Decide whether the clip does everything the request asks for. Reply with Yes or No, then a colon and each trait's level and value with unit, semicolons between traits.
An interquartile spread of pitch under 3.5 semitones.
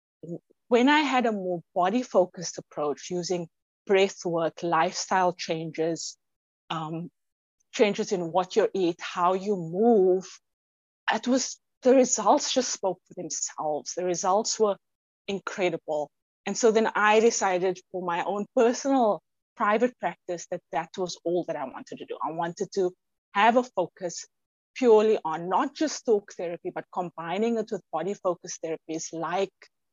No: average, 4.5 semitones